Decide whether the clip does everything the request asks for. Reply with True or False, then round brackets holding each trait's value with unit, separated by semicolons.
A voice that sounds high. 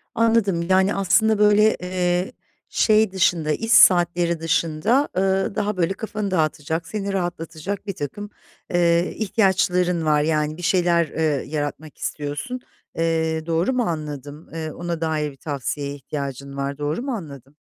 False (170 Hz)